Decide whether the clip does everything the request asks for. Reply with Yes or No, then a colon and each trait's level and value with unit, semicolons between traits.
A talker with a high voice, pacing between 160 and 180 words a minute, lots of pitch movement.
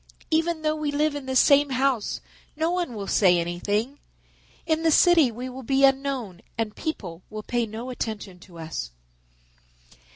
Yes: very high, 255 Hz; average, 165 wpm; wide, 6.0 semitones